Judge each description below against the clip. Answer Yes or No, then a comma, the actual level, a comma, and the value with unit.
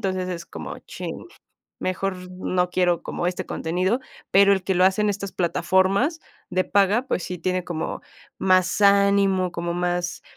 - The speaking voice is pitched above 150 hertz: Yes, medium, 185 Hz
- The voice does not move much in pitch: Yes, narrow, 1.8 semitones